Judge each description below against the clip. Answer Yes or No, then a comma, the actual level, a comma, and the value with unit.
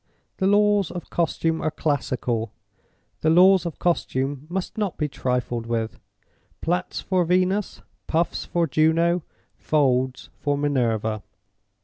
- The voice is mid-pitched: Yes, medium, 160 Hz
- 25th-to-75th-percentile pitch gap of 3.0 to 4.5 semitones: No, wide, 5.6 semitones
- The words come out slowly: Yes, slow, 120 wpm